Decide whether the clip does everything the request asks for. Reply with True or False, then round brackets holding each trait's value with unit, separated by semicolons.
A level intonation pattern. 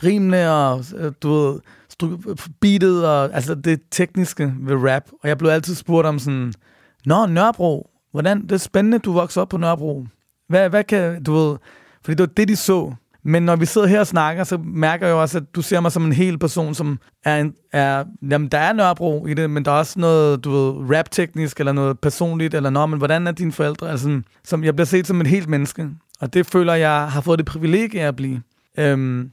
False (3.5 semitones)